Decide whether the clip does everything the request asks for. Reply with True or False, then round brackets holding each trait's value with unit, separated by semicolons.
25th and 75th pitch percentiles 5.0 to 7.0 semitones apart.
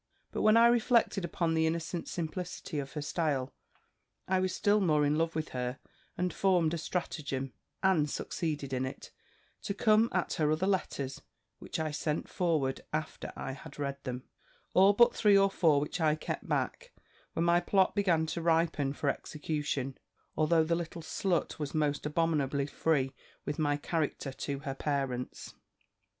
False (3.7 semitones)